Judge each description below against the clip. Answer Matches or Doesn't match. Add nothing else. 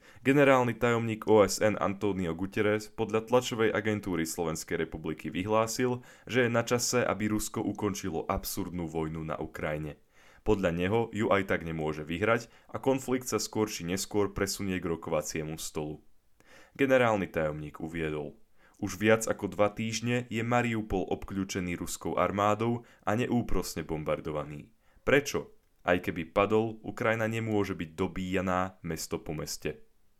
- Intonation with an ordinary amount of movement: Matches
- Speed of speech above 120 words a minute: Matches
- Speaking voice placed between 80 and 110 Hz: Matches